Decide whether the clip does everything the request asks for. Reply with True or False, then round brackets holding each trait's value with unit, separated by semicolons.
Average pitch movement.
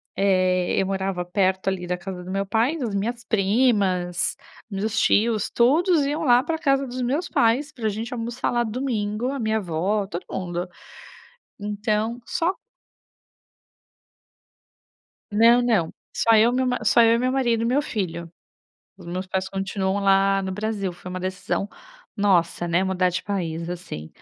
True (4.3 semitones)